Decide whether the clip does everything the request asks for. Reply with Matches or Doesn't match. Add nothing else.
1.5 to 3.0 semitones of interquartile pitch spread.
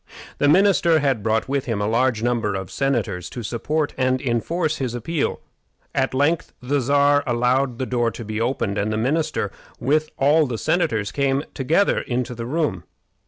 Doesn't match